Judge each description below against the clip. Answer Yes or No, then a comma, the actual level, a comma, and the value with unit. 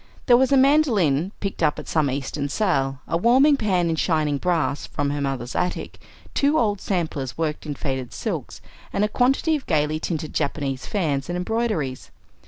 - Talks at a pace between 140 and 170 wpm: No, average, 180 wpm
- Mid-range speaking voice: Yes, medium, 160 Hz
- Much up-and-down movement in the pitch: Yes, wide, 6.9 semitones